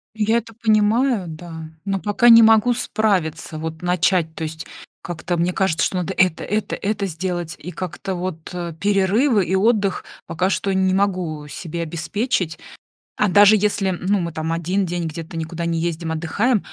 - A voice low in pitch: No, medium, 185 Hz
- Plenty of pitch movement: No, average, 3.7 semitones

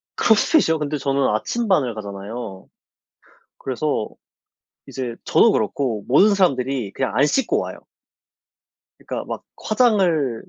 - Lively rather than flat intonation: Yes, wide, 7.7 semitones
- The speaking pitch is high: No, low, 135 Hz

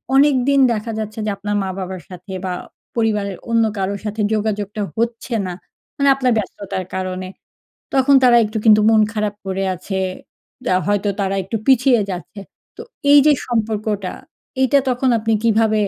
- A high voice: Yes, high, 215 Hz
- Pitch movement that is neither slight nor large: Yes, average, 3.2 semitones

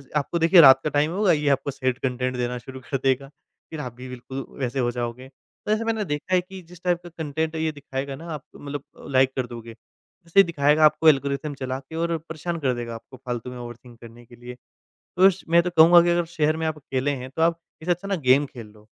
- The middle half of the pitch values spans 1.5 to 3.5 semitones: No, average, 4.5 semitones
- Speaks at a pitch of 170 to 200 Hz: No, medium, 140 Hz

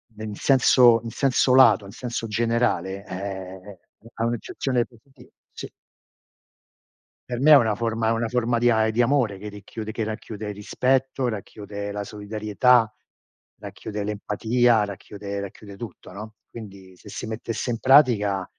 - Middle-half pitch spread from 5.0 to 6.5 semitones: No, average, 2.7 semitones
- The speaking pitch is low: Yes, low, 110 Hz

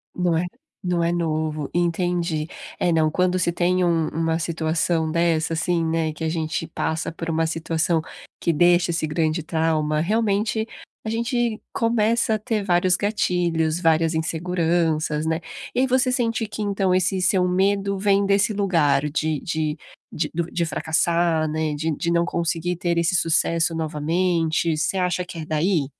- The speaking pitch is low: No, medium, 170 Hz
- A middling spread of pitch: No, narrow, 2.3 semitones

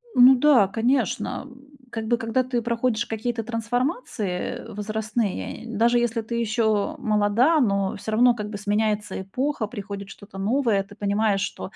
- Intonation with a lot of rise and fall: No, average, 2.8 semitones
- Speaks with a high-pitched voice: Yes, high, 225 Hz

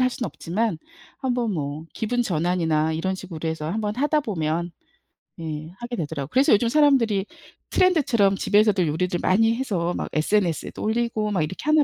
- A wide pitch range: Yes, wide, 6.4 semitones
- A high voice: Yes, high, 195 Hz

